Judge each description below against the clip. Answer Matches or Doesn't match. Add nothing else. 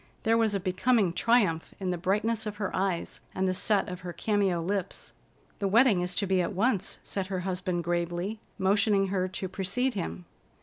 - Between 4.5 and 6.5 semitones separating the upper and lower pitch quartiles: Doesn't match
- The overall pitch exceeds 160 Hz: Matches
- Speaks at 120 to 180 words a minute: Doesn't match